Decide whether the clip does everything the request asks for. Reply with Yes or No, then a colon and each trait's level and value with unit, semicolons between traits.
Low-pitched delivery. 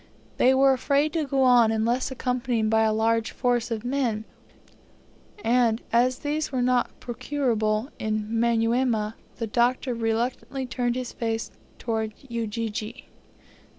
No: high, 235 Hz